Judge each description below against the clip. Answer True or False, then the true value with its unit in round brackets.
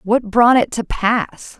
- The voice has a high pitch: True (225 Hz)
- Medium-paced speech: True (190 wpm)